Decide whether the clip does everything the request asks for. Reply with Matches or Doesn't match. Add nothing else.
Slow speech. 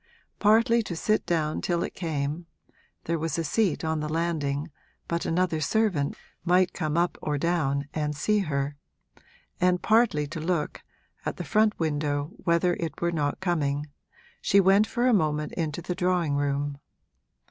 Doesn't match